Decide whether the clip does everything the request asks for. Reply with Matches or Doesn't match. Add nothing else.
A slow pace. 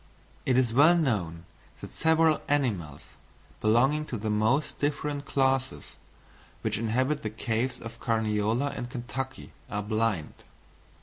Matches